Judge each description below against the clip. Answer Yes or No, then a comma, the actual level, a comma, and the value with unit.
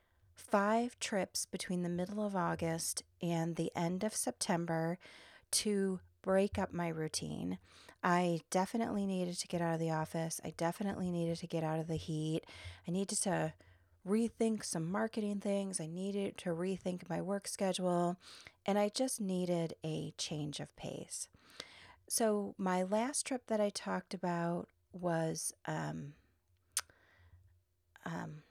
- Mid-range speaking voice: Yes, medium, 175 Hz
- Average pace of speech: Yes, average, 145 wpm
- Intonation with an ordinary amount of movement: Yes, average, 4.0 semitones